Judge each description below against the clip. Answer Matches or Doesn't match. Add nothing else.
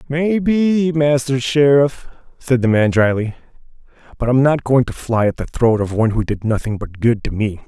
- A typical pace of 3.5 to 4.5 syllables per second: Doesn't match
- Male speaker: Matches